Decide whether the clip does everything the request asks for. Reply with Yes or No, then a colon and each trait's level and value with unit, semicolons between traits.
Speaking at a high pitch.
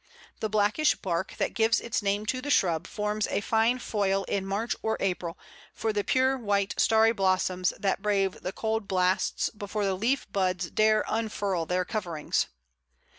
Yes: high, 205 Hz